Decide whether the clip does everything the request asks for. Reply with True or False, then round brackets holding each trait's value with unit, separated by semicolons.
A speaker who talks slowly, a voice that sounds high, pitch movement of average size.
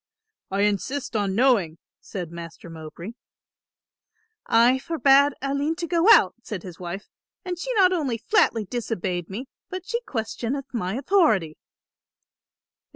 False (130 wpm; 235 Hz; 7.4 semitones)